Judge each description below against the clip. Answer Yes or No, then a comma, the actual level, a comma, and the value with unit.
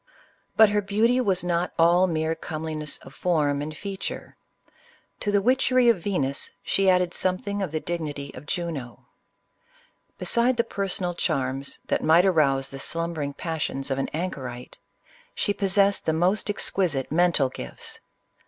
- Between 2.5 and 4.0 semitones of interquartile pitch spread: No, average, 5.0 semitones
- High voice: No, medium, 170 Hz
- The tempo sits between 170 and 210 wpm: No, average, 145 wpm